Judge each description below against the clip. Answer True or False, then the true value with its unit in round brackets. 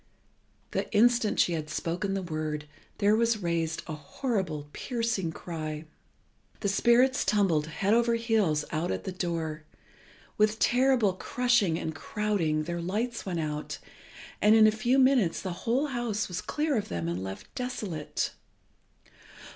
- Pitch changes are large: True (6.4 semitones)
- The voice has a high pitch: True (195 Hz)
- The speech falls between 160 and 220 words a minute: False (145 wpm)